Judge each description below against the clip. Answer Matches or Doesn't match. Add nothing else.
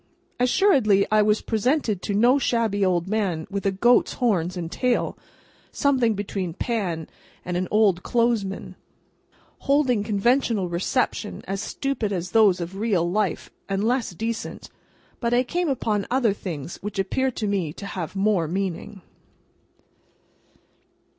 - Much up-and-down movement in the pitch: Doesn't match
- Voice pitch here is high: Matches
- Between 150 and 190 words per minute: Doesn't match